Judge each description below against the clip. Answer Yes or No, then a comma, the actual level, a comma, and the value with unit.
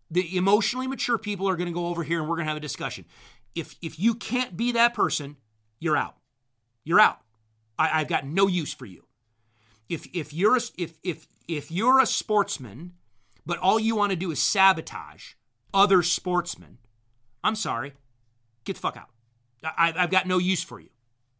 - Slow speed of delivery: No, average, 190 wpm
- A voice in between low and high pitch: Yes, medium, 165 Hz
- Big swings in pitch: Yes, wide, 7.7 semitones